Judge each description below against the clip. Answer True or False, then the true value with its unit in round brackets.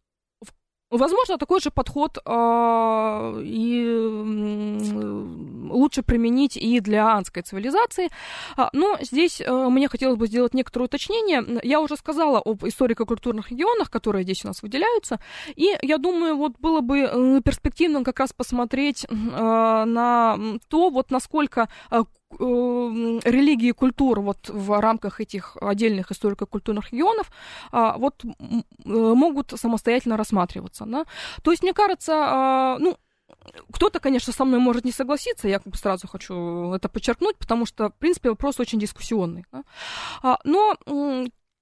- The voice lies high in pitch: True (245 Hz)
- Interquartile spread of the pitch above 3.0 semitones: True (4.8 semitones)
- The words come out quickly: False (130 wpm)